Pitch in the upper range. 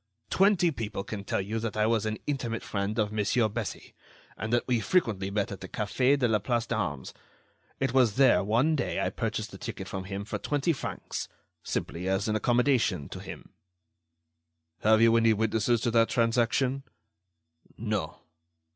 No: low, 110 Hz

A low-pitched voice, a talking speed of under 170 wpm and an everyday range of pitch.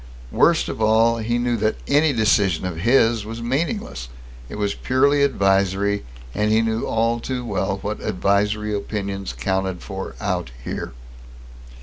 Yes: low, 110 Hz; average, 145 wpm; average, 3.1 semitones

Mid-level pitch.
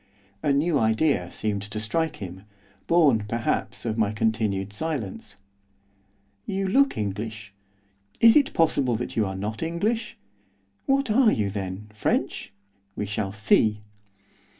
No: low, 110 Hz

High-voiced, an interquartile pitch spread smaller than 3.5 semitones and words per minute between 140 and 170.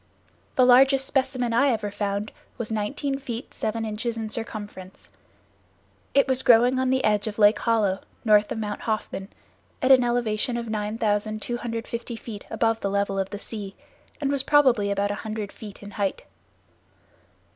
Yes: high, 220 Hz; average, 2.9 semitones; average, 160 wpm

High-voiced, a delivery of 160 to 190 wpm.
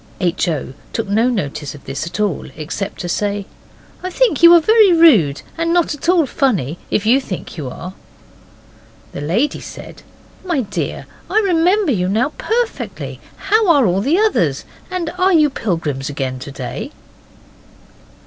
Yes: high, 225 Hz; average, 165 wpm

